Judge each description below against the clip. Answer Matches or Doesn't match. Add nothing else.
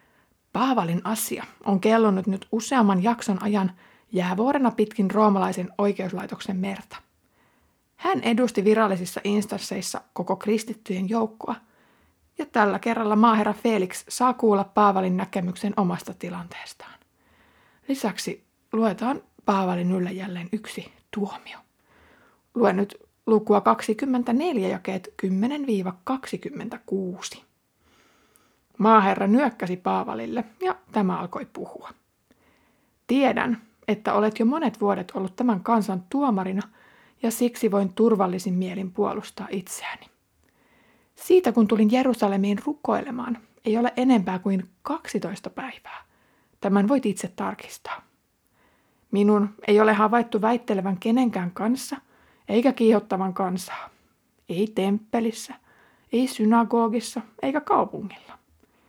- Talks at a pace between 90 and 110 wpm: Matches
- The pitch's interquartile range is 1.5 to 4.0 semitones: Matches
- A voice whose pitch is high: Matches